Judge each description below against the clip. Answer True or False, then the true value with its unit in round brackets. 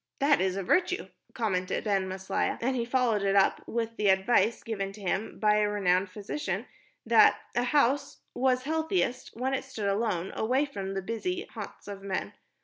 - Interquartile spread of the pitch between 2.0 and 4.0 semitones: False (4.7 semitones)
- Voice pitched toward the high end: True (215 Hz)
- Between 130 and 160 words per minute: False (180 wpm)